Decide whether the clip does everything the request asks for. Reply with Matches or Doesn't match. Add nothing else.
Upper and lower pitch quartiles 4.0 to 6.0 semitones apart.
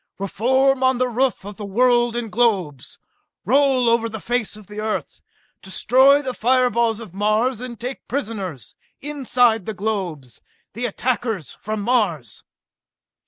Doesn't match